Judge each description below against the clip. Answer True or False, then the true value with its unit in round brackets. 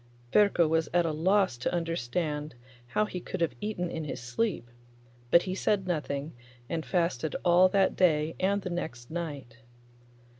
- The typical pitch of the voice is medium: True (170 Hz)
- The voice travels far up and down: False (3.7 semitones)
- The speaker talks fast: False (160 wpm)